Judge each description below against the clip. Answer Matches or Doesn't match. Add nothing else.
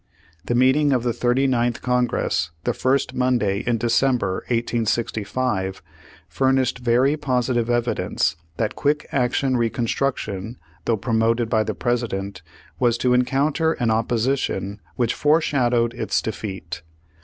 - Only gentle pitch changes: Matches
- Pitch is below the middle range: Matches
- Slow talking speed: Matches